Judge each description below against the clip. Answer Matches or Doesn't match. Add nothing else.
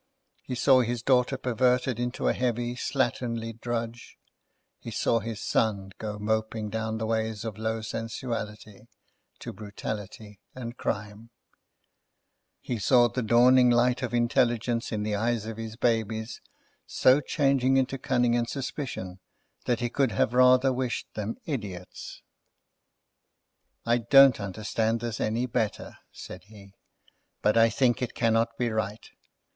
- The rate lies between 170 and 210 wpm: Doesn't match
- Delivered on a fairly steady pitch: Matches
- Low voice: Matches